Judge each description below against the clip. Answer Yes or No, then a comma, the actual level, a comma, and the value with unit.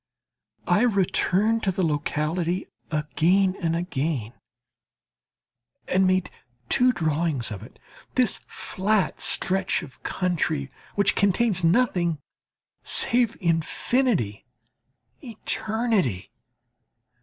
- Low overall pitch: No, medium, 180 Hz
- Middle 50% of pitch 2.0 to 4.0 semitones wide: No, average, 5.2 semitones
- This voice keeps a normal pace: No, slow, 85 wpm